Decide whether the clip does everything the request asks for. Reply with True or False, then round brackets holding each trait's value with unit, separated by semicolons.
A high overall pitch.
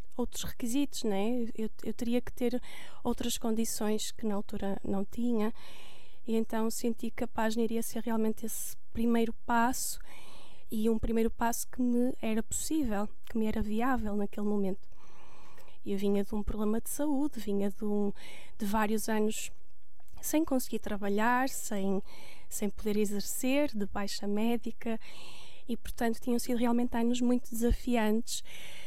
True (225 Hz)